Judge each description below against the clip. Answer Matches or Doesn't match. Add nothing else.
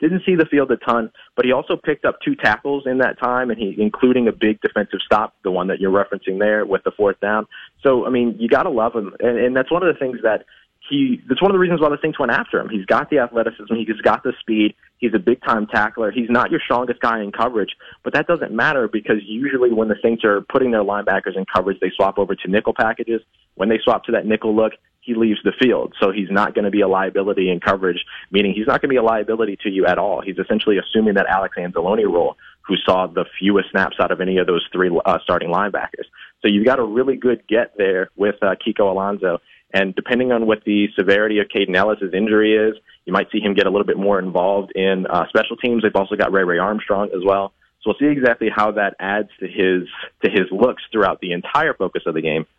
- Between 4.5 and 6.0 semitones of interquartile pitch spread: Doesn't match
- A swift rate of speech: Matches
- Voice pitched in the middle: Doesn't match